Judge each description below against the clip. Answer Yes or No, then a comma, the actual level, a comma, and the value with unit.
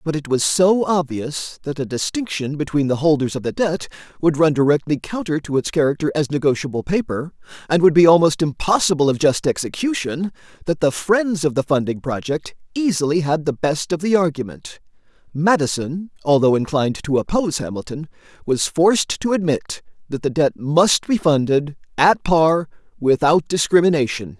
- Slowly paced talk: No, average, 160 wpm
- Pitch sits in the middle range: Yes, medium, 155 Hz